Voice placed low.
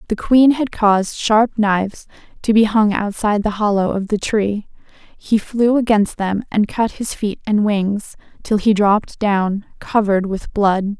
No: high, 210 Hz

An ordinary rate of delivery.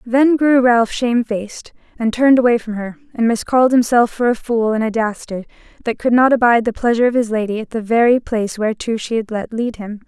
No: fast, 220 wpm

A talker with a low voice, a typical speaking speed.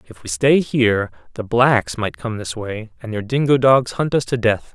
No: low, 115 Hz; fast, 230 wpm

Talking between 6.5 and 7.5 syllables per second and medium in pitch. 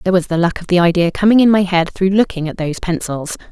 Yes: 6.6 syllables/s; medium, 180 Hz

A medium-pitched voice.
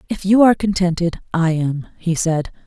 Yes: medium, 175 Hz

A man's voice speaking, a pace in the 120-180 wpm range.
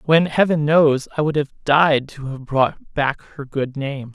No: male; fast, 205 wpm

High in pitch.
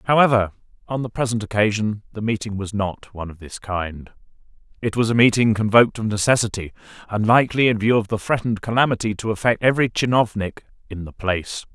No: low, 110 Hz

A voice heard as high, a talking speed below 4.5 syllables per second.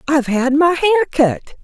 No: very high, 295 Hz; 5.9 syllables/s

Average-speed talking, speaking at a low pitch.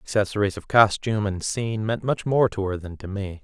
No: fast, 225 wpm; low, 105 Hz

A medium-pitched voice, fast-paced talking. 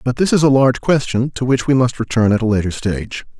No: low, 125 Hz; fast, 265 wpm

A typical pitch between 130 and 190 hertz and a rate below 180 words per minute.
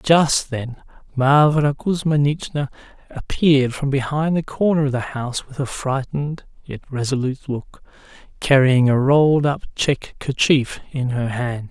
Yes: medium, 140 Hz; average, 140 wpm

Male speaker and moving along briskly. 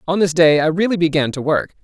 Yes: male; fast, 260 wpm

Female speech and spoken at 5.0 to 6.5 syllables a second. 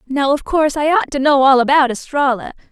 Yes: female; 5.8 syllables/s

